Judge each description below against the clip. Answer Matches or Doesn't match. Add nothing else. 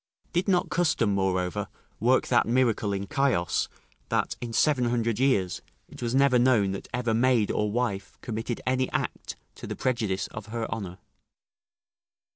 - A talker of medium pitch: Doesn't match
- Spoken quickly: Doesn't match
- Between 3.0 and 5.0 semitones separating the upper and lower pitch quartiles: Matches